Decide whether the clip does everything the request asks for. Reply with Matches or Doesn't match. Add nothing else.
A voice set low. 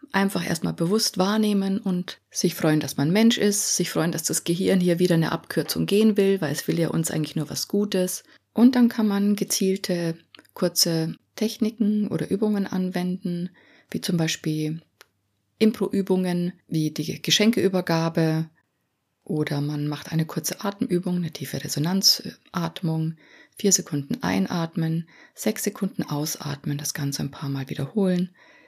Doesn't match